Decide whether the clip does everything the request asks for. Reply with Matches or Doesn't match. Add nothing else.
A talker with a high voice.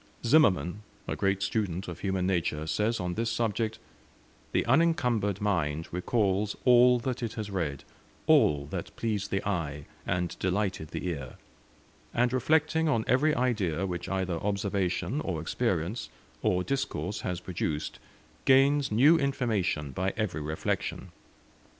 Doesn't match